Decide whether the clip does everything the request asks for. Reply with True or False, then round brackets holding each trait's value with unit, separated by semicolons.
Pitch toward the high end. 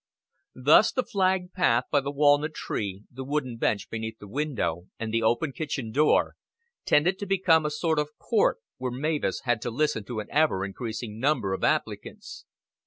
False (140 Hz)